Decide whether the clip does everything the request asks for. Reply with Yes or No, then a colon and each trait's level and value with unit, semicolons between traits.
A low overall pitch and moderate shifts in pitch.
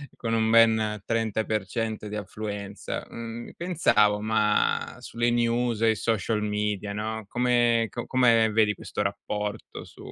No: low, 110 Hz; narrow, 1.7 semitones